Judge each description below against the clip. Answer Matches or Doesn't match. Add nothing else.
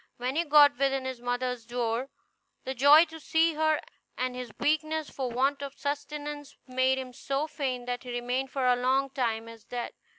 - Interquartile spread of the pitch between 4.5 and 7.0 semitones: Doesn't match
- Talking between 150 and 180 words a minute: Doesn't match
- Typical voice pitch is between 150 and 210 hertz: Doesn't match